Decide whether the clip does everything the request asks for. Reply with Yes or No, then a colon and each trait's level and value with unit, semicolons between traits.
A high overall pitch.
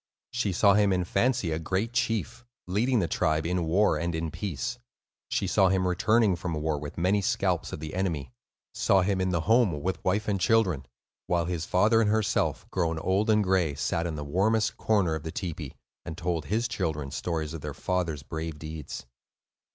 No: very low, 90 Hz